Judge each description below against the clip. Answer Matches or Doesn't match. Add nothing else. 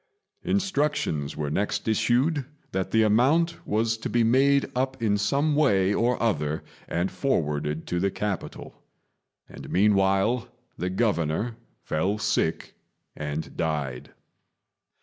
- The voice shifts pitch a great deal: Matches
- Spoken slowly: Matches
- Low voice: Matches